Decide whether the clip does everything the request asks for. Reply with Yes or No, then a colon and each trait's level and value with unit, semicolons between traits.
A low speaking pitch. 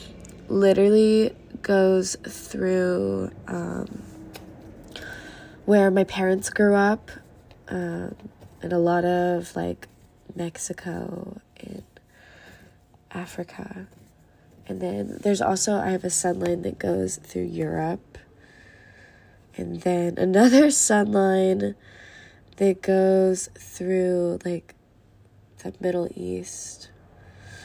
No: medium, 175 Hz